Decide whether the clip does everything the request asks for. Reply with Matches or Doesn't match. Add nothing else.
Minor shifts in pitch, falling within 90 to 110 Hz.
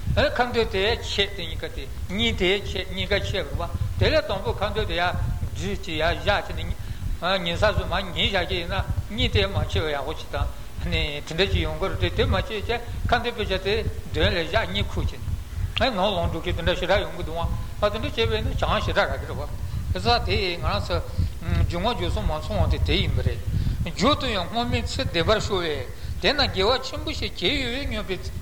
Matches